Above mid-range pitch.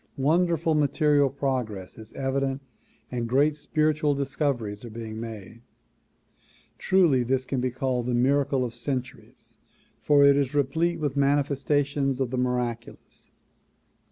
No: low, 135 Hz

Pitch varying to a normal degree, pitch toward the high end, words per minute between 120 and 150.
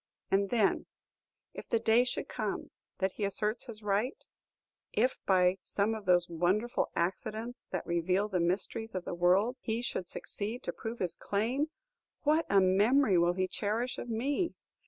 No: average, 4.0 semitones; high, 210 Hz; average, 165 wpm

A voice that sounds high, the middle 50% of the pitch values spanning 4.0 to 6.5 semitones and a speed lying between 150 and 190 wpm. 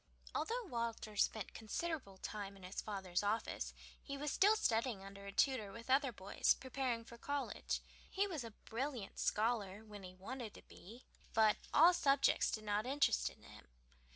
Yes: high, 230 Hz; average, 5.1 semitones; average, 165 wpm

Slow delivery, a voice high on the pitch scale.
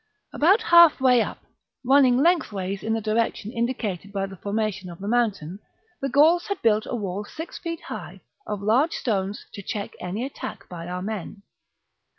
No: average, 175 wpm; high, 220 Hz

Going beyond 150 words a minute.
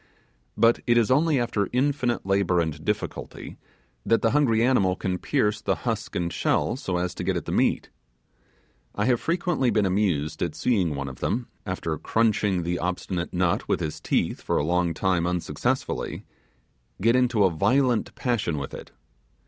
Yes: average, 175 wpm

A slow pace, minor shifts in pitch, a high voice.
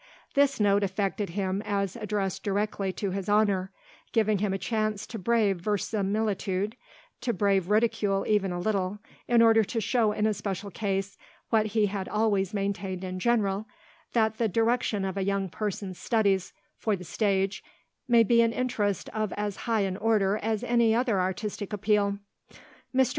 No: average, 165 wpm; narrow, 2.2 semitones; high, 205 Hz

